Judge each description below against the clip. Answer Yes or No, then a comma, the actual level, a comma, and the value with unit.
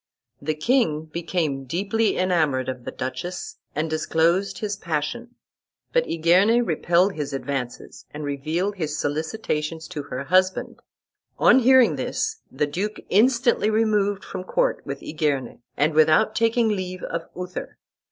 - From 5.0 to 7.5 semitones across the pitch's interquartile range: Yes, wide, 5.6 semitones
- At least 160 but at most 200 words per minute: No, slow, 135 wpm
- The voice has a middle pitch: Yes, medium, 170 Hz